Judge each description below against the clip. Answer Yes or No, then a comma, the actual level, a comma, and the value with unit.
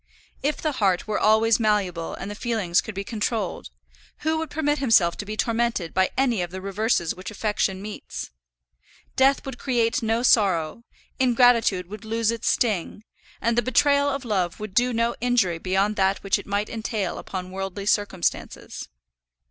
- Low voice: No, high, 215 Hz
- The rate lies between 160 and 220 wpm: Yes, average, 170 wpm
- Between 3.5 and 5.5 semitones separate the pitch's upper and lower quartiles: Yes, average, 3.8 semitones